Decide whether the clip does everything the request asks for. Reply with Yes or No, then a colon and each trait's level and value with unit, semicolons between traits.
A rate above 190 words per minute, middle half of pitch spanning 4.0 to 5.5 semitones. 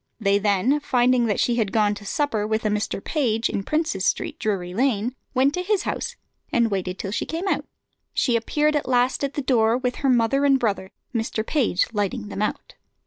Yes: fast, 205 wpm; average, 4.5 semitones